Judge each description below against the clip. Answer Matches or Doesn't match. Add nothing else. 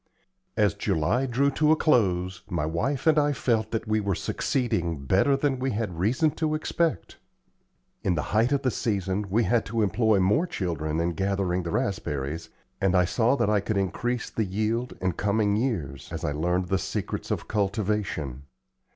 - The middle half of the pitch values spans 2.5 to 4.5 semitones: Doesn't match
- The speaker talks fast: Doesn't match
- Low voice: Matches